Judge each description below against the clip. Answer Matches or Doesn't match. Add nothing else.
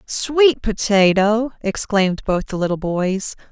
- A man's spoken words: Doesn't match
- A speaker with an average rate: Doesn't match